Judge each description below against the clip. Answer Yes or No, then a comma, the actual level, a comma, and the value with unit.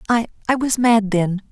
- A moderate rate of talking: Yes, average, 160 wpm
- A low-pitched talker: No, high, 220 Hz